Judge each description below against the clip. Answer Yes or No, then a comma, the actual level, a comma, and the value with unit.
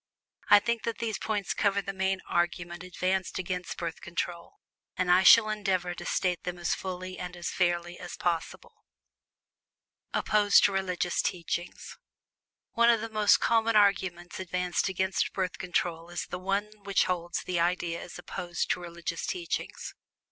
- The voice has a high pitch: No, medium, 180 Hz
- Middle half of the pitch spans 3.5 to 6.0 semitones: No, narrow, 2.4 semitones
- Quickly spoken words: No, average, 160 wpm